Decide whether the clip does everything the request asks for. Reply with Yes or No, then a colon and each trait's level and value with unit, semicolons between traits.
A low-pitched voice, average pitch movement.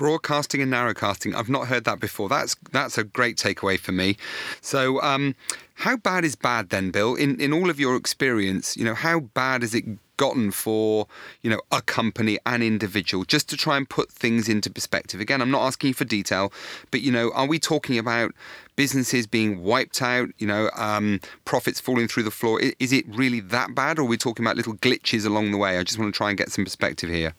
Yes: low, 115 Hz; average, 3.9 semitones